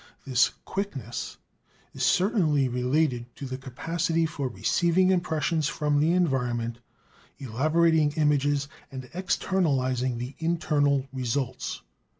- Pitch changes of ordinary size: Yes, average, 4.1 semitones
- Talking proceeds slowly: Yes, slow, 105 wpm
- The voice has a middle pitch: Yes, medium, 145 Hz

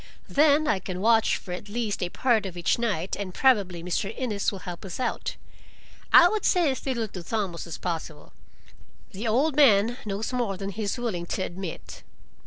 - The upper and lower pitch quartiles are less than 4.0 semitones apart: No, average, 4.8 semitones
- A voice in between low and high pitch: No, high, 205 Hz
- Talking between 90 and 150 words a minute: No, average, 195 wpm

